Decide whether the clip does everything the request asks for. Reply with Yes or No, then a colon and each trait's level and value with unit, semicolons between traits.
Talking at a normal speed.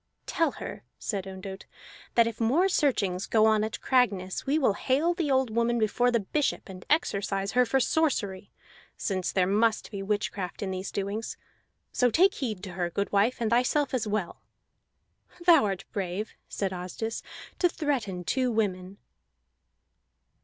Yes: average, 155 wpm